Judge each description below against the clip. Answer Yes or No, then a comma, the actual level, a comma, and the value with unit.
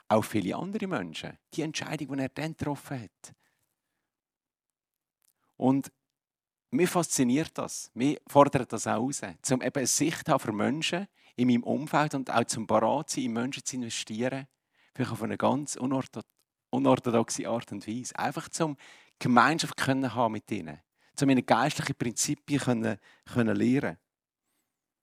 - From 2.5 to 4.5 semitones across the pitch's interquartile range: Yes, average, 3.6 semitones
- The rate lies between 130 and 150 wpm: Yes, average, 145 wpm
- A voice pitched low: Yes, low, 130 Hz